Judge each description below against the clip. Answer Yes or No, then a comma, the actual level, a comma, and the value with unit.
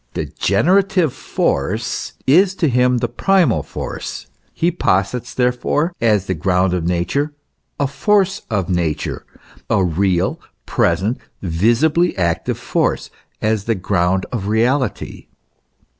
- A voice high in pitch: No, low, 115 Hz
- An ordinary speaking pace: No, slow, 120 wpm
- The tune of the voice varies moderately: No, wide, 8.2 semitones